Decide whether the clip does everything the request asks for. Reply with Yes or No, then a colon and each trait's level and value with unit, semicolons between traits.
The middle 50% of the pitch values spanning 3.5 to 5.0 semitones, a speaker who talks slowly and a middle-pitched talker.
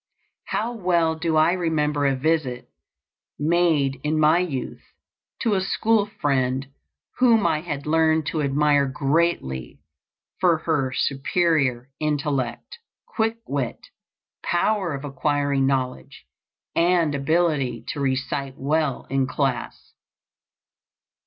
Yes: average, 3.8 semitones; slow, 110 wpm; medium, 150 Hz